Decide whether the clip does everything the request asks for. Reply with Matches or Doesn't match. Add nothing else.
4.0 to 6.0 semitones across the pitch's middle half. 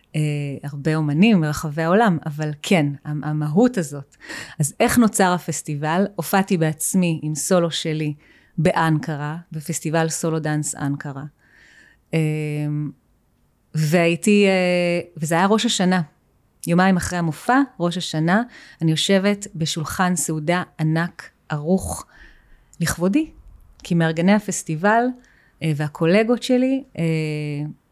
Doesn't match